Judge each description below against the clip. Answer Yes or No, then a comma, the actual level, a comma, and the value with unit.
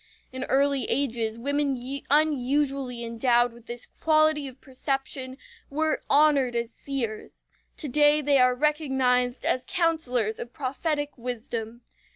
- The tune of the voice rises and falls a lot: No, average, 3.2 semitones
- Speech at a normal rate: No, slow, 125 wpm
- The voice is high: Yes, very high, 265 Hz